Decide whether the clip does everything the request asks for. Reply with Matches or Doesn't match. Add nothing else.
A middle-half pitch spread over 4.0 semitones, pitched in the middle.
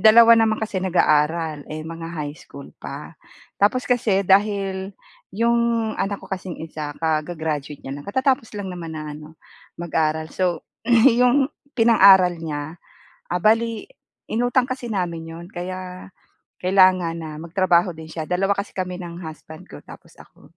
Matches